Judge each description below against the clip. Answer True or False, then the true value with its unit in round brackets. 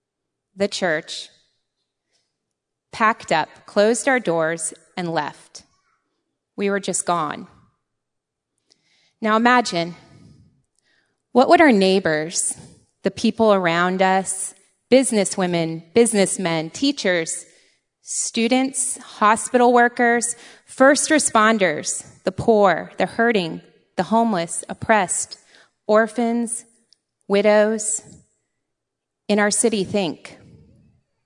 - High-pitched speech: True (205 Hz)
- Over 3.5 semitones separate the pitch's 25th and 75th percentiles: True (4.3 semitones)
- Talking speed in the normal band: False (85 wpm)